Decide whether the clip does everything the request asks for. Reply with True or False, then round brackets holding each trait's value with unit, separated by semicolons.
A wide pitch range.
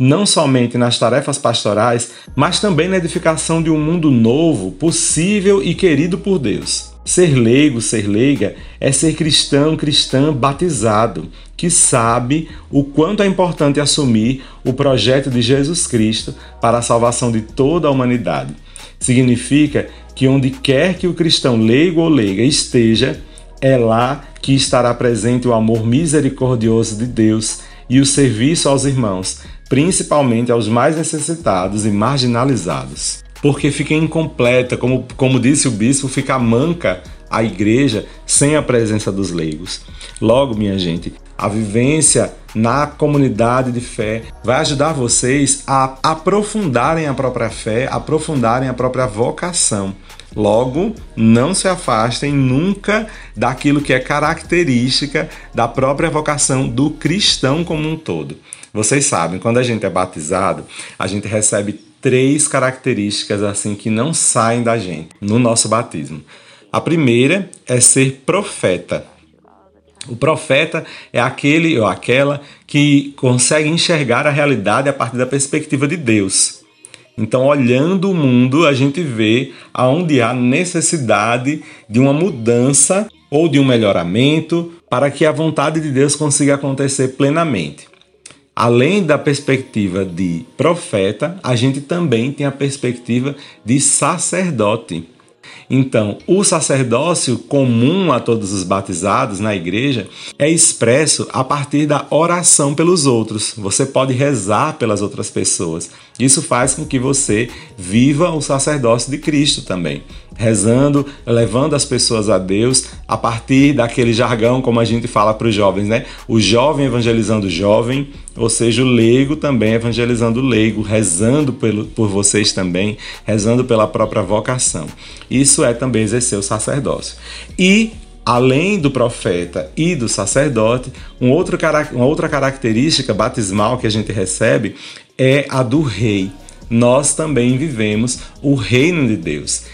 False (4.6 semitones)